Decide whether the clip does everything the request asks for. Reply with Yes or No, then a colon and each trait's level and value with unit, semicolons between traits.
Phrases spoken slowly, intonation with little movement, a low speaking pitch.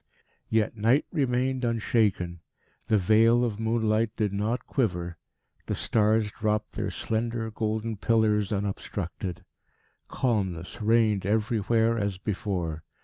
Yes: slow, 110 wpm; narrow, 2.1 semitones; low, 110 Hz